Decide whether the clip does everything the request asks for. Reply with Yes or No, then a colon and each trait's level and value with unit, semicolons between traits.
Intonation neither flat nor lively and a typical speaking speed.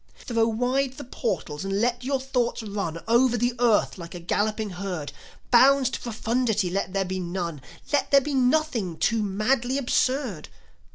Yes: average, 4.8 semitones; average, 165 wpm